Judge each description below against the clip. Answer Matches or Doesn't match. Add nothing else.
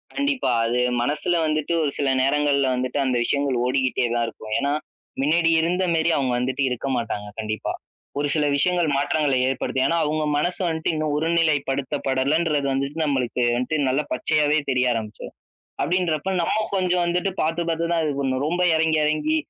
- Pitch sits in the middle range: Matches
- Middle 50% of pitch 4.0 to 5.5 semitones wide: Doesn't match